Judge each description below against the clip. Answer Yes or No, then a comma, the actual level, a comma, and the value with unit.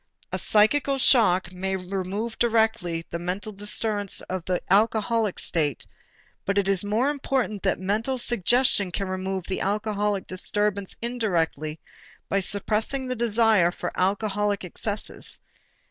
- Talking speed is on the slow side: Yes, slow, 130 wpm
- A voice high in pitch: Yes, high, 205 Hz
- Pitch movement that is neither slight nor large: Yes, average, 3.0 semitones